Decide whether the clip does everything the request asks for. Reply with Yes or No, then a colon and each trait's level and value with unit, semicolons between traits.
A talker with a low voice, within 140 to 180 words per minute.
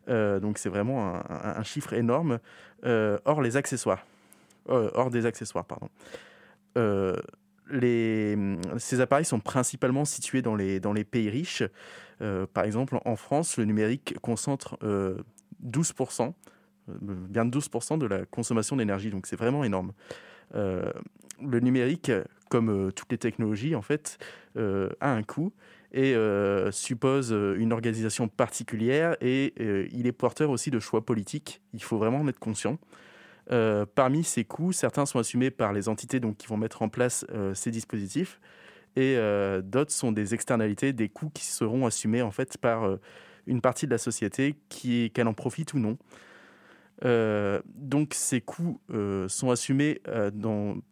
Yes: low, 120 Hz; average, 165 wpm